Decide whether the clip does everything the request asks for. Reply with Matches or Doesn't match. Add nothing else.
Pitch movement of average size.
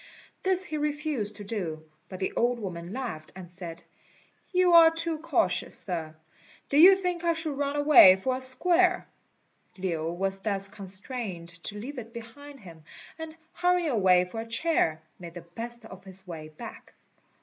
Doesn't match